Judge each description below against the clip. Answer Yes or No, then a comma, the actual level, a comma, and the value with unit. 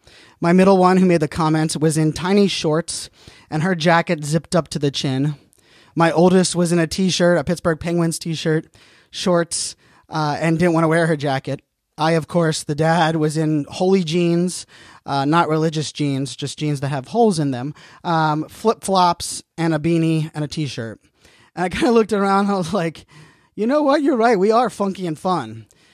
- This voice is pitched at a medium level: Yes, medium, 165 Hz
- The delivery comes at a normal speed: No, fast, 210 wpm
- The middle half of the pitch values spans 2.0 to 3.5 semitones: Yes, average, 2.8 semitones